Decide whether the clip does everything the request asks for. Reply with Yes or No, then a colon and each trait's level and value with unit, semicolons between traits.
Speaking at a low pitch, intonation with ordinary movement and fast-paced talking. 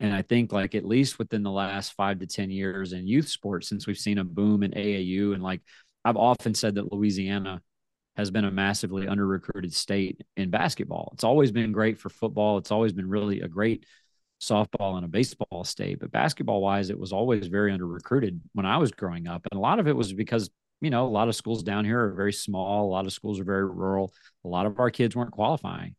No: low, 100 Hz; narrow, 1.9 semitones; fast, 230 wpm